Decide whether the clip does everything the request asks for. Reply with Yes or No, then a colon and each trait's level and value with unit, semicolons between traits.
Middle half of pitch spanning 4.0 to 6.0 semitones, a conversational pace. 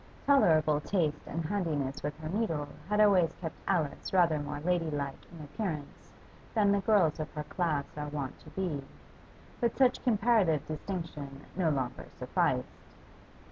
Yes: average, 4.6 semitones; average, 145 wpm